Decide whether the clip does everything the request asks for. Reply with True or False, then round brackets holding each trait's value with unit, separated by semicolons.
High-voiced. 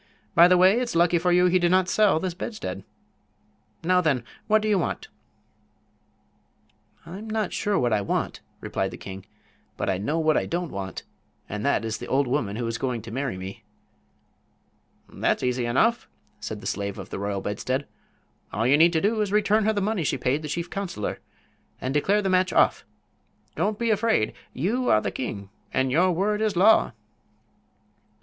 False (170 Hz)